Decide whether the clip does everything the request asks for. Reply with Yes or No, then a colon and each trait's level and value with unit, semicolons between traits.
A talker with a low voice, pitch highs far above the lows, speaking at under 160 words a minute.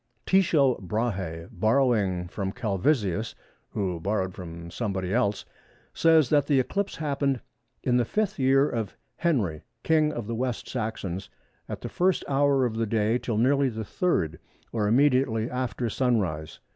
Yes: low, 115 Hz; wide, 5.7 semitones; average, 145 wpm